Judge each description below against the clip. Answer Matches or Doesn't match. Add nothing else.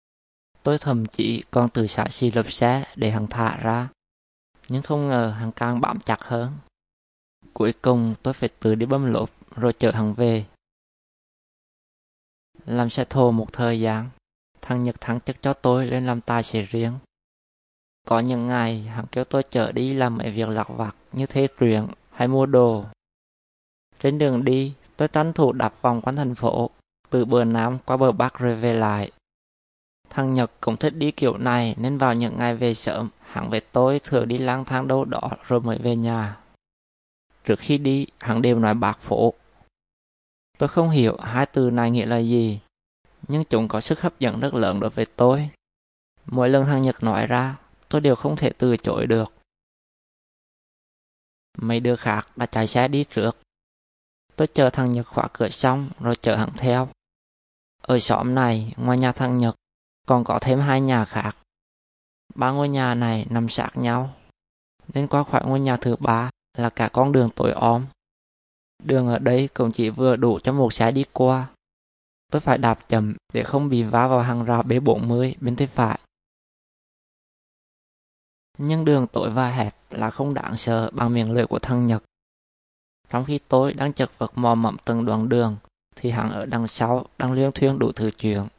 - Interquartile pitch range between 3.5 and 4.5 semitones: Doesn't match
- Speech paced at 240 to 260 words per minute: Doesn't match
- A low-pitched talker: Matches